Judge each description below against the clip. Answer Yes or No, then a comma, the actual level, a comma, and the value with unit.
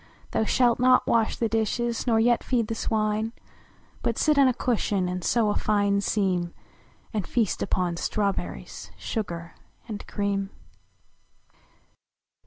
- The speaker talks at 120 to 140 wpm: Yes, slow, 135 wpm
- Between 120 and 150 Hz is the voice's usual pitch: No, high, 215 Hz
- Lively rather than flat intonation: No, average, 2.8 semitones